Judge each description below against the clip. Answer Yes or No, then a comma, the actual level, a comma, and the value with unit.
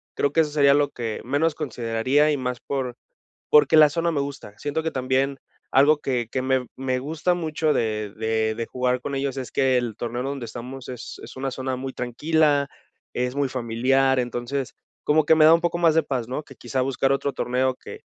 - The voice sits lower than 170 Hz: Yes, low, 135 Hz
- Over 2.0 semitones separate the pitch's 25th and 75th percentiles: Yes, average, 2.8 semitones